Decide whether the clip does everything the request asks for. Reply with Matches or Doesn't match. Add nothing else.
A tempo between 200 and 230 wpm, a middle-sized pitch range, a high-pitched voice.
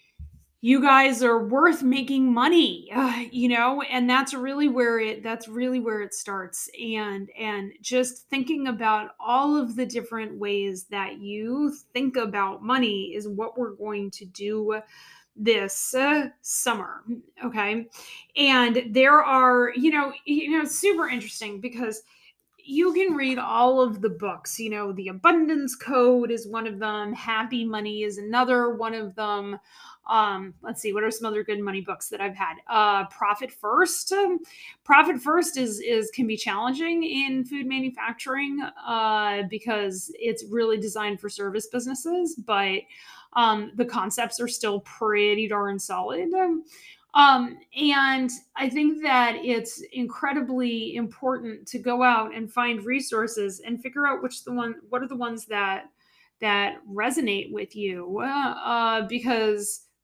Doesn't match